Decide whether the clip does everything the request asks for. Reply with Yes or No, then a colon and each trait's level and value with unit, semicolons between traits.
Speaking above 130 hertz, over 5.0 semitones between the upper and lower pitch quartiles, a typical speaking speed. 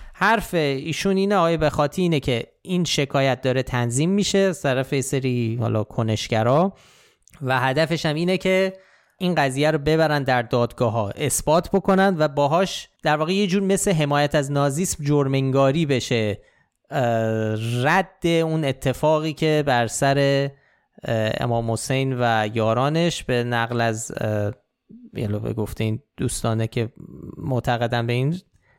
Yes: medium, 140 Hz; wide, 5.5 semitones; average, 135 wpm